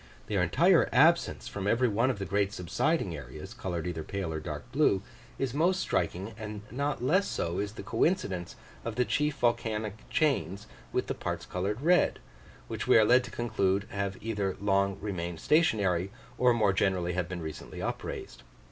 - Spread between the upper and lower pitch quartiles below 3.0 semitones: No, average, 4.8 semitones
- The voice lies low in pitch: Yes, low, 100 Hz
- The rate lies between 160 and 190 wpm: Yes, average, 175 wpm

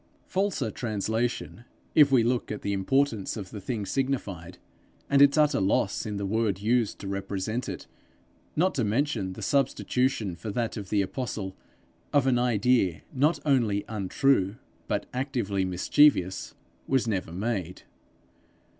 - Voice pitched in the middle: No, low, 110 Hz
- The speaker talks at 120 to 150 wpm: Yes, average, 145 wpm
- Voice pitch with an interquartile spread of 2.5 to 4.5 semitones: No, average, 5.2 semitones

